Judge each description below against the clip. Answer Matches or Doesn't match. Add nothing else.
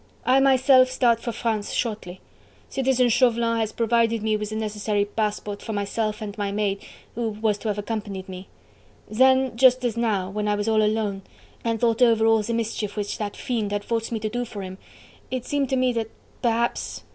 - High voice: Matches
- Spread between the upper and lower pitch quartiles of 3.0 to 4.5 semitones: Doesn't match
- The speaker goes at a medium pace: Matches